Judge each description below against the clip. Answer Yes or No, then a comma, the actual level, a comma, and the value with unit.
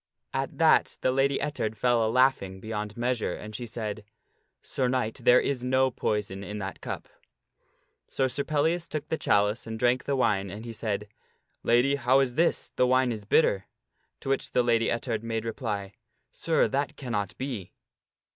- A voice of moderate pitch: No, low, 120 Hz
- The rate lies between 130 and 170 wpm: No, average, 185 wpm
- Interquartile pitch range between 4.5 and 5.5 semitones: No, average, 3.7 semitones